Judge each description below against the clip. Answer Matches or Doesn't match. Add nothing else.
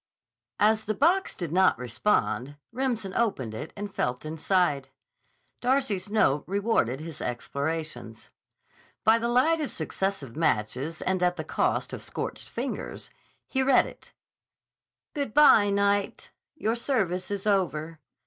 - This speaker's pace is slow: Matches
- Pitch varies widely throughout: Matches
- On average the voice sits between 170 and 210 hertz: Matches